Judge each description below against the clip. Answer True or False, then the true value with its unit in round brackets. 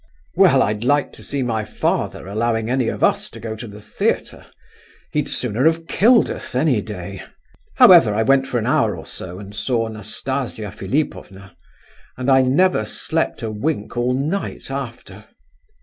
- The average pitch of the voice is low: True (120 Hz)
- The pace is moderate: True (165 wpm)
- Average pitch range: True (4.4 semitones)